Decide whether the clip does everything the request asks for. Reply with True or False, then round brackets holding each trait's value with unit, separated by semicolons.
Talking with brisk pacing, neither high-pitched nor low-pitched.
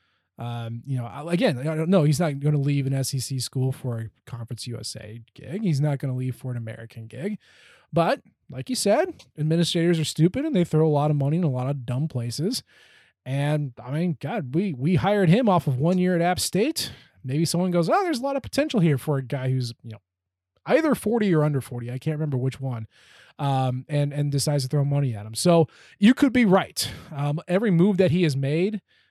True (225 wpm; 150 Hz)